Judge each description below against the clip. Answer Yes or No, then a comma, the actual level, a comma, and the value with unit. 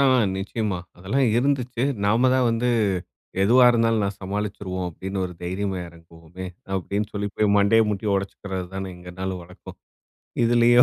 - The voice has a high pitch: No, low, 100 Hz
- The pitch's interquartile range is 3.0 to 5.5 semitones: Yes, average, 3.5 semitones